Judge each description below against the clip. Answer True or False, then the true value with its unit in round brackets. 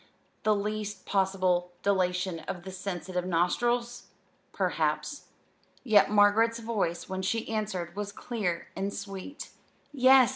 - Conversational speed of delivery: False (115 wpm)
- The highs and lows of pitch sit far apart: False (3.1 semitones)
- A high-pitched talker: True (200 Hz)